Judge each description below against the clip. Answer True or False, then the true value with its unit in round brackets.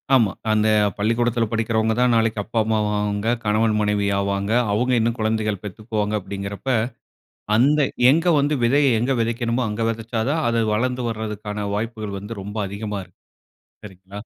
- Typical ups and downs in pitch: False (2.2 semitones)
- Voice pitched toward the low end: True (110 Hz)